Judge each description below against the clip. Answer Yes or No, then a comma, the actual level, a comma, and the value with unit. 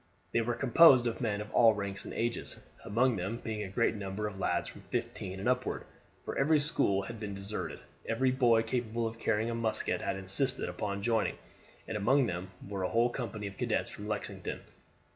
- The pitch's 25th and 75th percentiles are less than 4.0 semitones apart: Yes, average, 3.1 semitones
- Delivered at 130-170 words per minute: No, average, 200 wpm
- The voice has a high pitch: No, low, 110 Hz